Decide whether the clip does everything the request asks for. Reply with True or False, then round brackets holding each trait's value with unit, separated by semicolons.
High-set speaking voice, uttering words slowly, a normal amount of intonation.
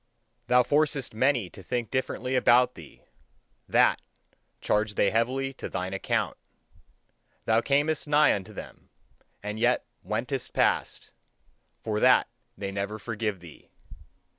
False (115 Hz; 125 wpm; 4.0 semitones)